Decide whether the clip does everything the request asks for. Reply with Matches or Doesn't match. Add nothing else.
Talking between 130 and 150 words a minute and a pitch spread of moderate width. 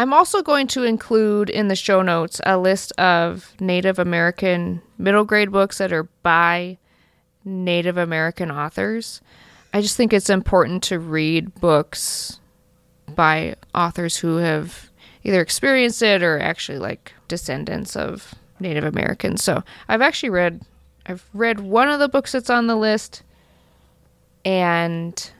Matches